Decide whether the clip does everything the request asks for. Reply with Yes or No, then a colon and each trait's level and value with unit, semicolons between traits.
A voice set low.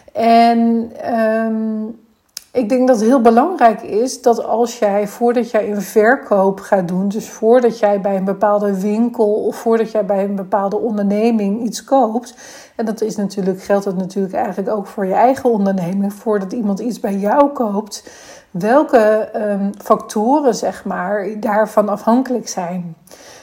No: high, 220 Hz